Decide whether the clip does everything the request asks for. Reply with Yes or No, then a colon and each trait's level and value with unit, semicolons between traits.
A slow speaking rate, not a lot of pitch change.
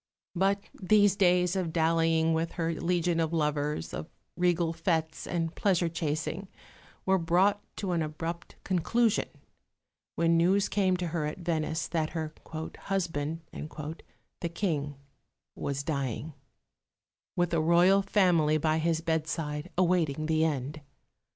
Yes: slow, 130 wpm; narrow, 2.3 semitones